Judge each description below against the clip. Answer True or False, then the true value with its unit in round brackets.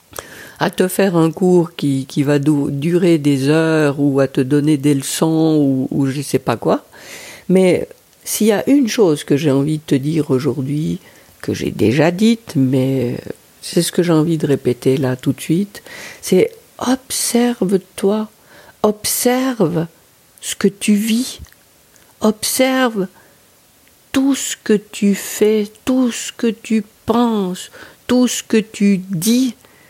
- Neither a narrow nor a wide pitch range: False (7.2 semitones)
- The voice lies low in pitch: False (180 Hz)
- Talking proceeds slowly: False (155 wpm)